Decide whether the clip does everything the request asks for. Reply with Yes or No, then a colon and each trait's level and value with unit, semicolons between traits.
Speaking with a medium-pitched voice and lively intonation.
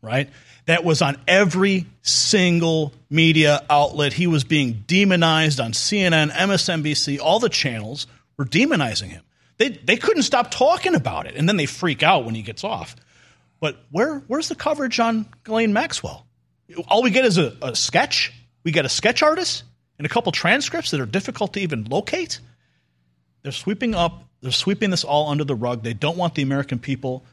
Yes: medium, 160 Hz; wide, 7.1 semitones